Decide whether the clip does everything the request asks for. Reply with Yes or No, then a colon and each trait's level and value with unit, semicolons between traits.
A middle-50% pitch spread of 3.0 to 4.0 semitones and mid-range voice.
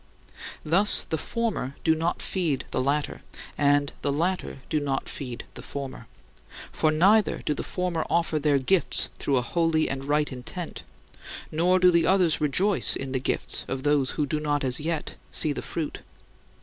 Yes: average, 3.5 semitones; medium, 150 Hz